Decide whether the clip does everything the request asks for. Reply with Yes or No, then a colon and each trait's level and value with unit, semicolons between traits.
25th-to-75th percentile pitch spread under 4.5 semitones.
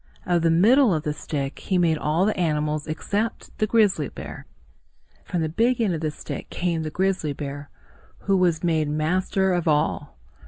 Yes: average, 3.8 semitones